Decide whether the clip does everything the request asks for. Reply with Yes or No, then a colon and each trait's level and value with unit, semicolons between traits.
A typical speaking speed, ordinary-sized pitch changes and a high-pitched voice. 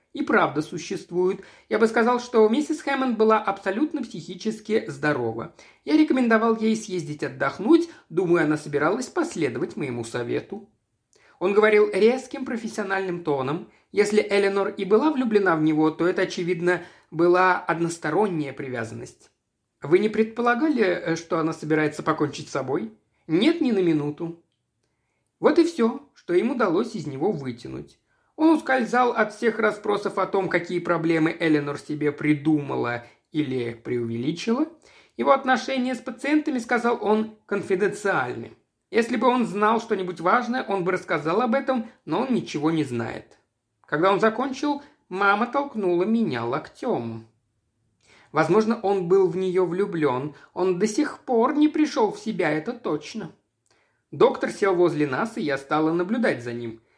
No: average, 140 wpm; wide, 7.1 semitones; high, 195 Hz